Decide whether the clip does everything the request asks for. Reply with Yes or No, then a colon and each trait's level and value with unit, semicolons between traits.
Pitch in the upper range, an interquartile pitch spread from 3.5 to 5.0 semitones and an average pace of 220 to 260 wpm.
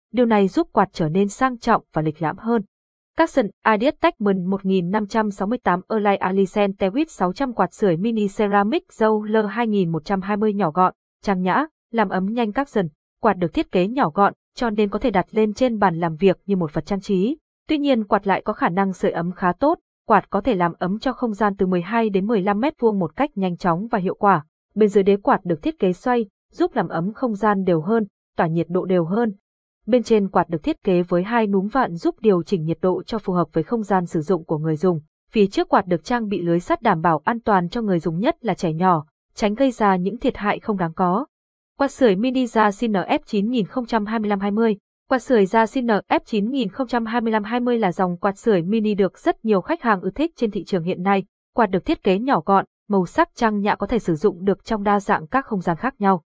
Yes: high, 205 Hz; average, 4.0 semitones; average, 230 wpm